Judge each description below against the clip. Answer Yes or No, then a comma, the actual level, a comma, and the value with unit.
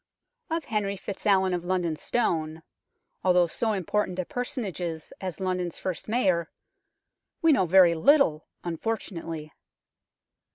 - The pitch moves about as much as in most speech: Yes, average, 3.7 semitones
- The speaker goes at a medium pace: No, slow, 115 wpm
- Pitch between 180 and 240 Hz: Yes, medium, 185 Hz